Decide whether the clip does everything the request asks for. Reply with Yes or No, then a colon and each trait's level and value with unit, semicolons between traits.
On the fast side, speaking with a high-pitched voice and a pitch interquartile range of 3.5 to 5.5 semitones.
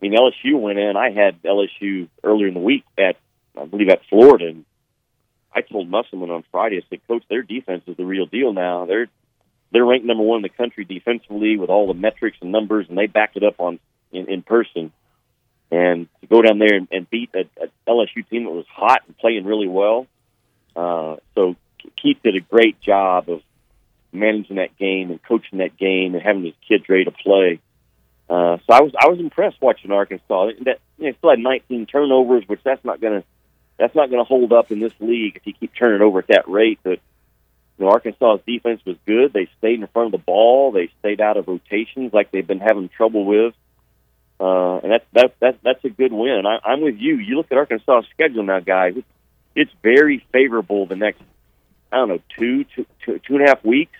No: fast, 220 wpm; low, 105 Hz; average, 4.4 semitones